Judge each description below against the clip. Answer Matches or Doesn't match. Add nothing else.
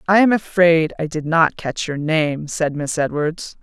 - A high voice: Doesn't match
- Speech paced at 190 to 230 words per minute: Matches